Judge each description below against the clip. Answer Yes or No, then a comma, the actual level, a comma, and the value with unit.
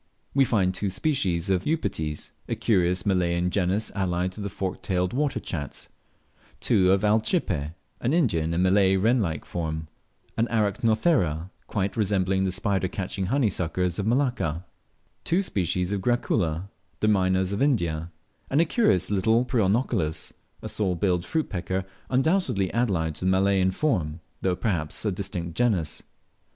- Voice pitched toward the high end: No, very low, 95 Hz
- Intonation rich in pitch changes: No, average, 3.9 semitones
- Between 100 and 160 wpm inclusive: Yes, average, 150 wpm